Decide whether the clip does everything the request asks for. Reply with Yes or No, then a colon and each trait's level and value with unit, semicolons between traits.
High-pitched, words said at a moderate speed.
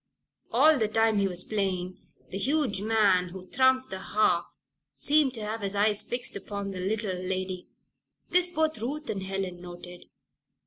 Yes: high, 205 Hz; average, 165 wpm